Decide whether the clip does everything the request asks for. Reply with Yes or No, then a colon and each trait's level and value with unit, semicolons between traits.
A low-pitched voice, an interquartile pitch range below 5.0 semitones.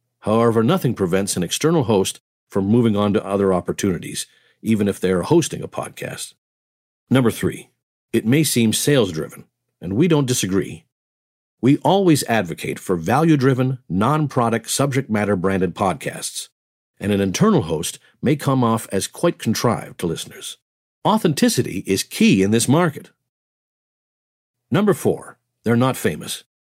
No: low, 110 Hz; wide, 5.4 semitones